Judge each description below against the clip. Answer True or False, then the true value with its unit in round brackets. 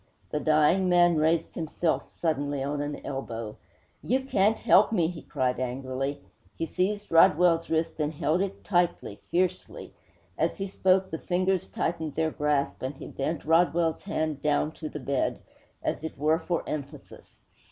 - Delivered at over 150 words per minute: True (160 wpm)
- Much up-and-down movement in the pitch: False (3.4 semitones)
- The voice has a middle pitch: True (160 Hz)